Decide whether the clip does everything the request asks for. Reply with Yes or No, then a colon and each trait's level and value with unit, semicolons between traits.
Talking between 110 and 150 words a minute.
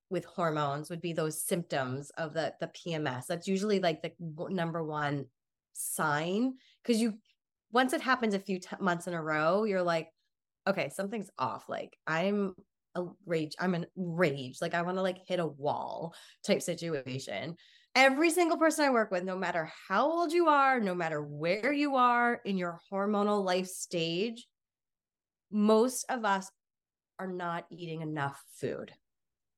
No: average, 165 wpm